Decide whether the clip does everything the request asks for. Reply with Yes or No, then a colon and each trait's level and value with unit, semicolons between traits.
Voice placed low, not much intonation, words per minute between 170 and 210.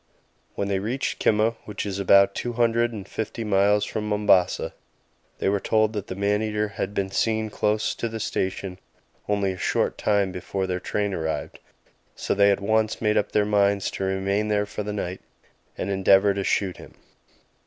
Yes: low, 100 Hz; narrow, 1.6 semitones; average, 185 wpm